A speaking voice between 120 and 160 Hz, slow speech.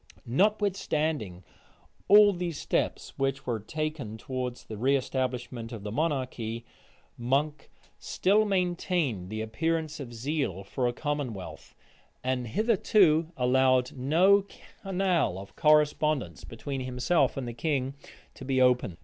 Yes: low, 135 Hz; slow, 115 wpm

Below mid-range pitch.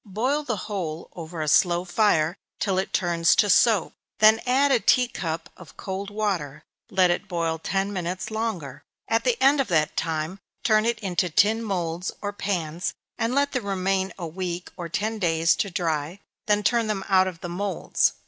No: high, 190 Hz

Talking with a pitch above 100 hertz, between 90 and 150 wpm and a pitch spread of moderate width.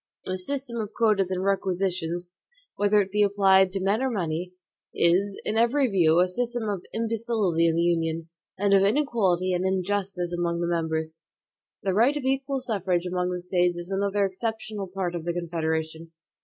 No: high, 190 Hz; average, 175 wpm; average, 3.3 semitones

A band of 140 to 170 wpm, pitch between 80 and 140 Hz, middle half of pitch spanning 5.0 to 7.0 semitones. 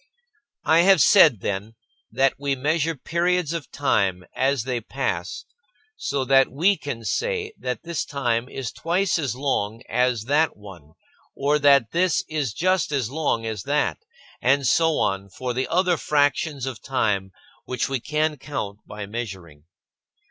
Yes: average, 155 wpm; low, 135 Hz; wide, 5.5 semitones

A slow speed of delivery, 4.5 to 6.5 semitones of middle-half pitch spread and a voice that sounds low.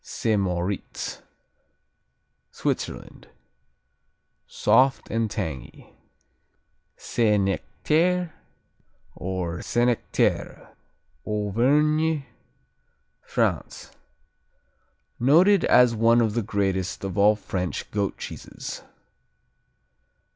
Yes: slow, 70 wpm; average, 5.1 semitones; low, 110 Hz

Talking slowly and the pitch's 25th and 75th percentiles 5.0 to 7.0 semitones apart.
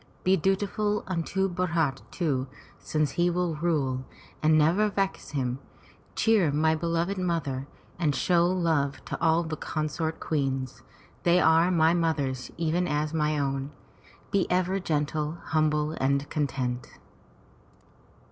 No: slow, 130 wpm; average, 3.3 semitones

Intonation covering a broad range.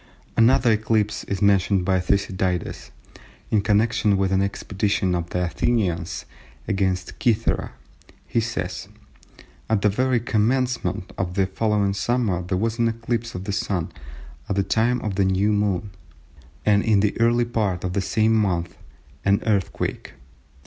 No: average, 2.9 semitones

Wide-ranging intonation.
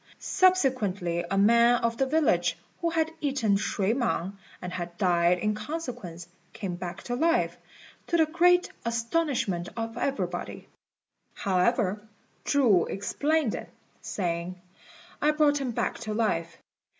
Yes: wide, 7.7 semitones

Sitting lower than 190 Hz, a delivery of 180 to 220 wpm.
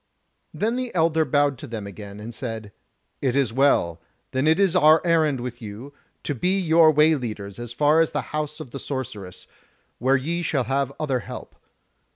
Yes: medium, 140 Hz; average, 190 wpm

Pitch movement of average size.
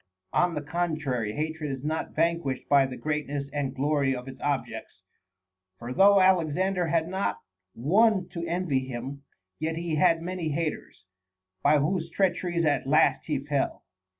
Yes: average, 3.6 semitones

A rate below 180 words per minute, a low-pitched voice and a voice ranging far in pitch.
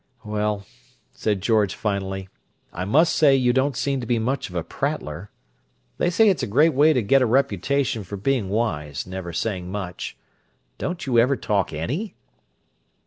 Yes: average, 170 wpm; low, 110 Hz; wide, 6.1 semitones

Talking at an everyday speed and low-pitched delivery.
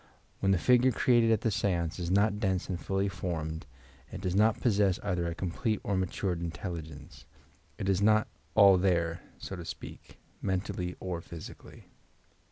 Yes: average, 170 wpm; very low, 95 Hz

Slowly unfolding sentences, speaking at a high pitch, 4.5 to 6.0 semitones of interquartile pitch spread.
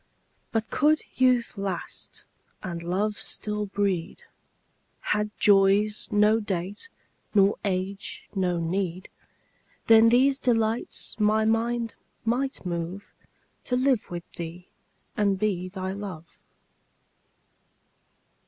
No: slow, 100 wpm; high, 205 Hz; average, 3.3 semitones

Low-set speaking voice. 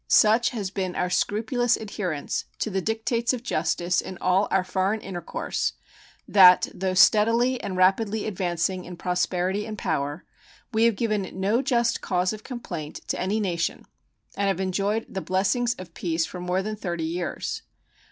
No: high, 195 Hz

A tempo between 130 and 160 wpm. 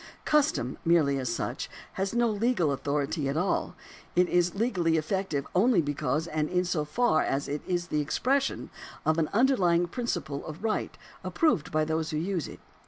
No: average, 170 wpm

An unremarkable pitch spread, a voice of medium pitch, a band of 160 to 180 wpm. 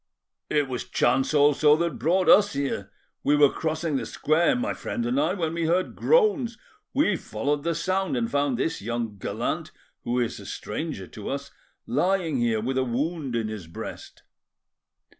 No: wide, 5.8 semitones; medium, 145 Hz; average, 175 wpm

